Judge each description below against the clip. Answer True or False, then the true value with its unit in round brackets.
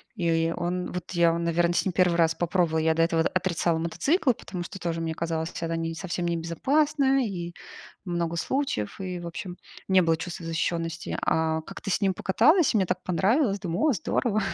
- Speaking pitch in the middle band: True (175 Hz)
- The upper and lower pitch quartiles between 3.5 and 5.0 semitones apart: False (2.6 semitones)